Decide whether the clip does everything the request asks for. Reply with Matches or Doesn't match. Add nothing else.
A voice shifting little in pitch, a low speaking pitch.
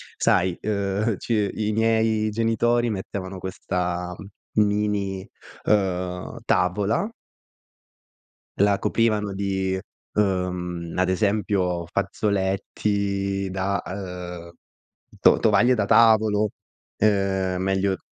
Matches